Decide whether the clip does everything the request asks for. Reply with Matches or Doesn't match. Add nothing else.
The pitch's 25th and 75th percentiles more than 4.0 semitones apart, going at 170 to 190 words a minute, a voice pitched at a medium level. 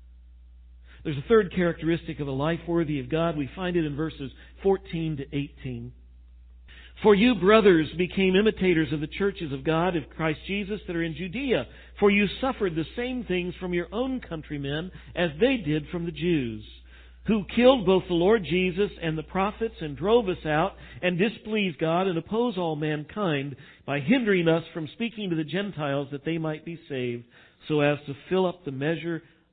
Matches